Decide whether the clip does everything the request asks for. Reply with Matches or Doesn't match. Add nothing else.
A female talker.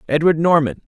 Doesn't match